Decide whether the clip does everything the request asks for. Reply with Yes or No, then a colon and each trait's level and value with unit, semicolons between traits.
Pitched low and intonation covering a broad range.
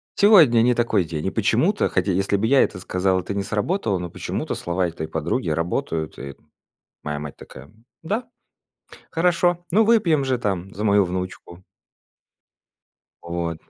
Yes: very low, 95 Hz; wide, 7.4 semitones